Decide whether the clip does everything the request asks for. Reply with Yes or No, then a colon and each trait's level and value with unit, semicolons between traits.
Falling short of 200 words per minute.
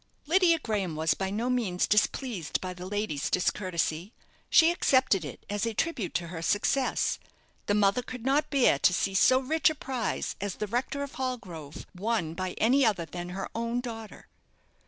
Yes: average, 180 wpm